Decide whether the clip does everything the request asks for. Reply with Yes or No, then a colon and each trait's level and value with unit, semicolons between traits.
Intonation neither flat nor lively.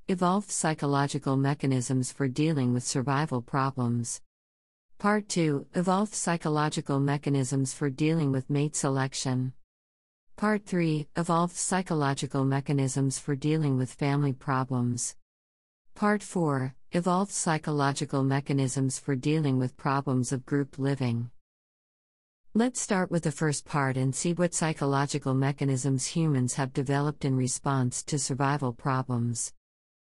Yes: average, 3.1 semitones